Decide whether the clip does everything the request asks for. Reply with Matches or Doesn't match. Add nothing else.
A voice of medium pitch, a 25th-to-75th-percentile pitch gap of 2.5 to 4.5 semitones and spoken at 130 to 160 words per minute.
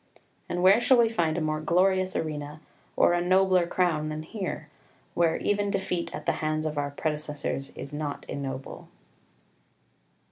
Matches